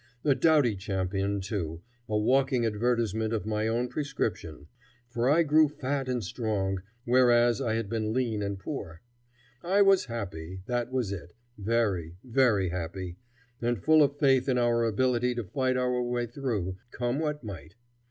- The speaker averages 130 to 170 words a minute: Yes, average, 160 wpm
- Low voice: Yes, low, 115 Hz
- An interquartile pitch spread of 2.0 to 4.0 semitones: No, average, 4.4 semitones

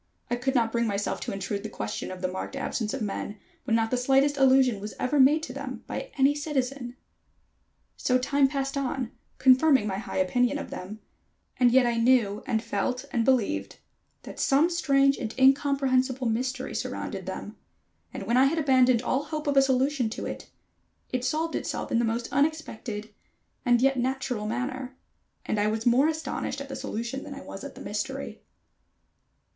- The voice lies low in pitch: No, very high, 255 Hz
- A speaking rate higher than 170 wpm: Yes, average, 185 wpm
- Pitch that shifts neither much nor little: Yes, average, 3.2 semitones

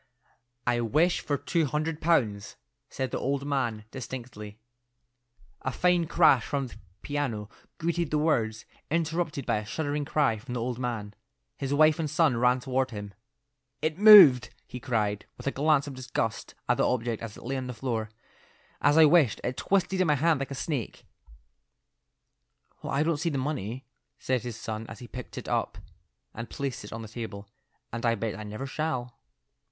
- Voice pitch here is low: Yes, low, 130 Hz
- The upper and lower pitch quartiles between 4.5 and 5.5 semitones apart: Yes, average, 4.8 semitones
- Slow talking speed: No, average, 185 wpm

